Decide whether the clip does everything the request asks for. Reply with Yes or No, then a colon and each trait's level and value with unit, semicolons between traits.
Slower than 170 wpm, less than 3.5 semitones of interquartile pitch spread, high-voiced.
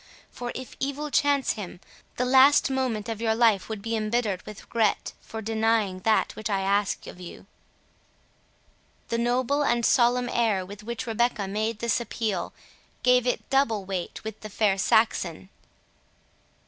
Yes: average, 155 wpm; average, 3.0 semitones; high, 225 Hz